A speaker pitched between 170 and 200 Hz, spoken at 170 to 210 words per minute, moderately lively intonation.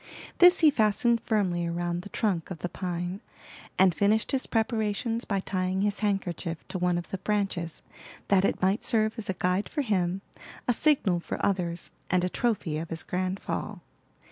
Yes: high, 190 Hz; average, 180 wpm; average, 3.4 semitones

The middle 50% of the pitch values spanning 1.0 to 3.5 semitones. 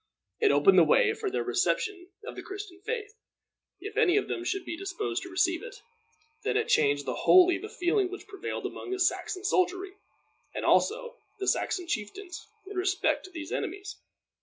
Yes: narrow, 2.6 semitones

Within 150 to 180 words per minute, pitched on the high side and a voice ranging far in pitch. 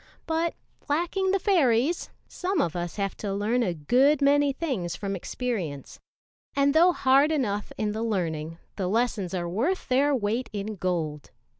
Yes: average, 160 wpm; high, 230 Hz; wide, 7.6 semitones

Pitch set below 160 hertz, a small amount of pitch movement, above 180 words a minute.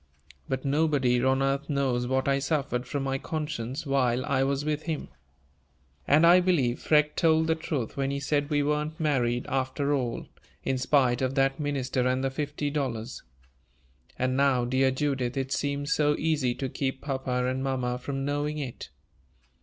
No: low, 135 Hz; narrow, 2.2 semitones; average, 170 wpm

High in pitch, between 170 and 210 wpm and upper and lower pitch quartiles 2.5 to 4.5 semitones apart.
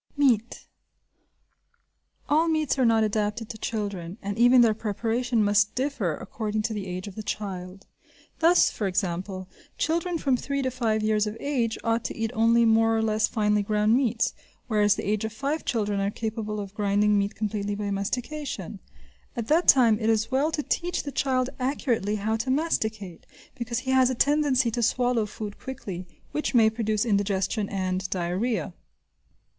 Yes: high, 220 Hz; average, 175 wpm; average, 3.5 semitones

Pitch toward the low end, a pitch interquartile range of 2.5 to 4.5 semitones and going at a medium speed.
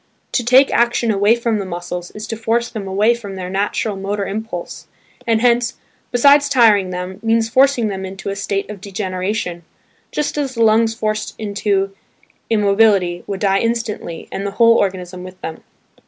No: high, 210 Hz; average, 3.1 semitones; average, 170 wpm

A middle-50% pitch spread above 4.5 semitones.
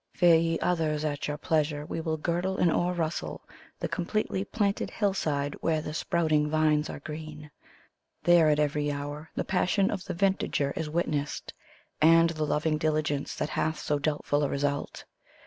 No: narrow, 2.4 semitones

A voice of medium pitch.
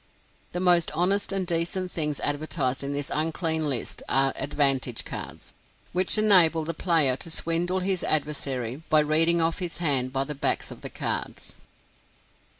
Yes: medium, 160 Hz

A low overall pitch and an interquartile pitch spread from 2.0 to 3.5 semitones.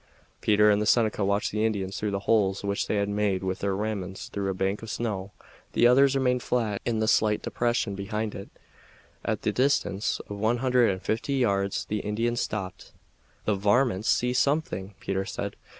Yes: low, 105 Hz; average, 3.0 semitones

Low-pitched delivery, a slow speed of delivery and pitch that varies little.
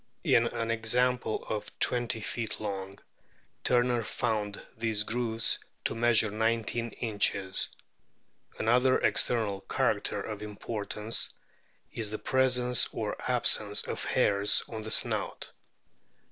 Yes: low, 115 Hz; slow, 110 wpm; narrow, 2.1 semitones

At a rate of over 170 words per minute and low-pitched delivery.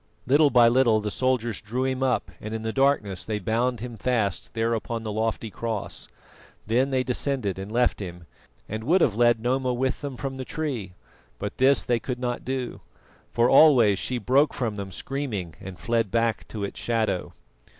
Yes: average, 190 wpm; low, 120 Hz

